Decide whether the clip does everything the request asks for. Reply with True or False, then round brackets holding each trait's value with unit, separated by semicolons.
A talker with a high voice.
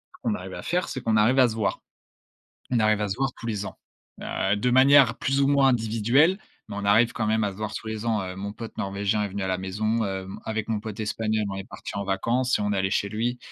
False (110 Hz)